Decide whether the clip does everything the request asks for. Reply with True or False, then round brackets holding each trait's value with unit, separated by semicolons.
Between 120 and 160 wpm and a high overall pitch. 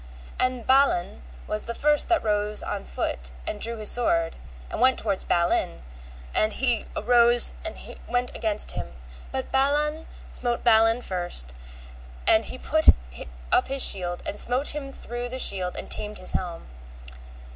True (155 wpm; 235 Hz)